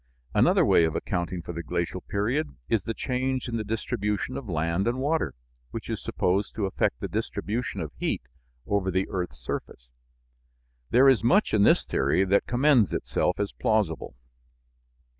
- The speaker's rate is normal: Yes, average, 165 wpm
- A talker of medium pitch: No, low, 105 Hz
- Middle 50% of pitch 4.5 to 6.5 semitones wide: Yes, wide, 5.4 semitones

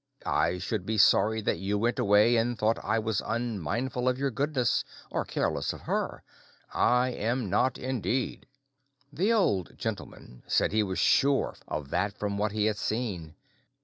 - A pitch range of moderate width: Yes, average, 3.5 semitones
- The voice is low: Yes, low, 110 Hz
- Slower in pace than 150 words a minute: No, average, 165 wpm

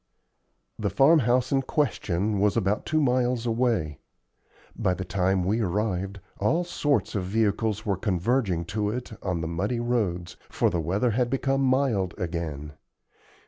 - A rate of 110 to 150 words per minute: Yes, average, 145 wpm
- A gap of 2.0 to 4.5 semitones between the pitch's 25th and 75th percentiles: No, average, 5.3 semitones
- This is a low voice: Yes, low, 105 Hz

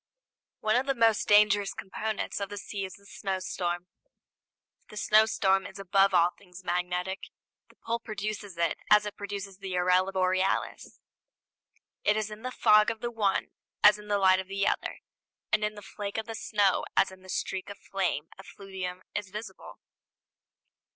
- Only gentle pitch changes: Yes, narrow, 2.1 semitones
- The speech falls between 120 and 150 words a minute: No, average, 170 wpm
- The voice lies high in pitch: Yes, high, 200 Hz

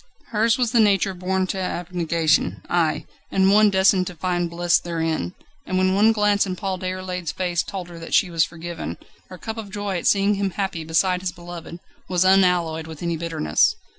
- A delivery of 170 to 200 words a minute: Yes, average, 195 wpm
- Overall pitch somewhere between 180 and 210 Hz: Yes, medium, 185 Hz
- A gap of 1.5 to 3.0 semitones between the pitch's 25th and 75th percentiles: Yes, narrow, 2.4 semitones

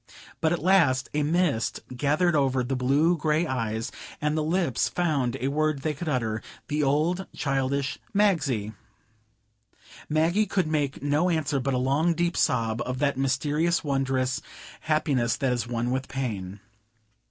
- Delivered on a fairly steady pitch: No, average, 3.6 semitones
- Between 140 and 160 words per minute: Yes, average, 150 wpm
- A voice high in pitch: No, medium, 140 Hz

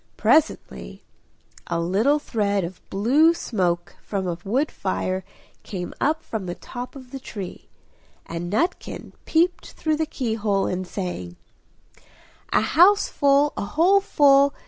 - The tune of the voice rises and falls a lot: Yes, wide, 8.0 semitones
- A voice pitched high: Yes, high, 220 Hz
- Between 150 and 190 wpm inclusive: No, average, 140 wpm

